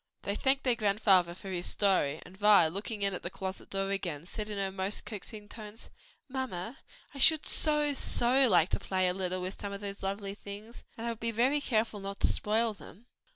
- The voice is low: No, high, 200 Hz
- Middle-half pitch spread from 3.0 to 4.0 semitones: Yes, average, 3.3 semitones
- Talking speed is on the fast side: Yes, fast, 215 wpm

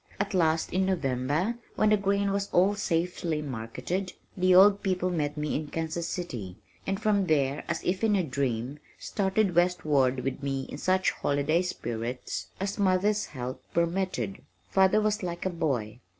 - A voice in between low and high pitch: Yes, medium, 175 Hz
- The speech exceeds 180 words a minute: No, average, 165 wpm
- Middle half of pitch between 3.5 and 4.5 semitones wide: No, wide, 5.4 semitones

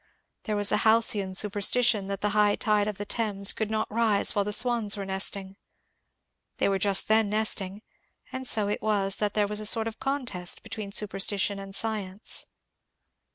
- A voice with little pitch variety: Yes, narrow, 1.8 semitones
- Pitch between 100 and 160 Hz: No, high, 210 Hz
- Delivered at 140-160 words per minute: No, average, 180 wpm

